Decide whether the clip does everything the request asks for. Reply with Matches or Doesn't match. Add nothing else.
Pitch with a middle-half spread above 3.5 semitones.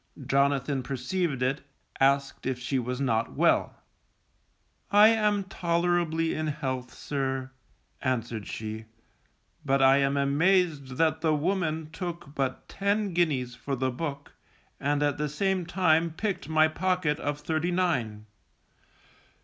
Matches